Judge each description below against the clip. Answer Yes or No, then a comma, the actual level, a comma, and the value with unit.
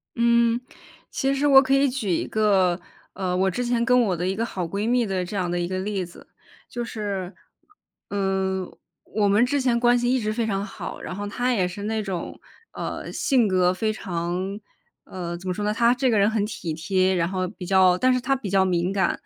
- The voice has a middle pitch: No, high, 200 Hz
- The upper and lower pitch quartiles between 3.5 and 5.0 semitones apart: Yes, average, 4.1 semitones